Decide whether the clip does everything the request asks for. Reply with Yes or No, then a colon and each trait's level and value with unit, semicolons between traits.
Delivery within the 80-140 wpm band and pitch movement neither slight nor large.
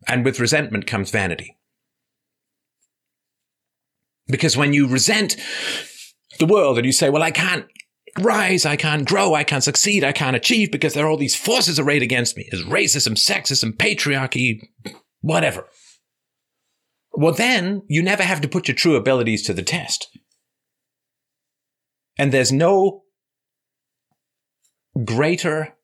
Yes: slow, 135 wpm; average, 3.6 semitones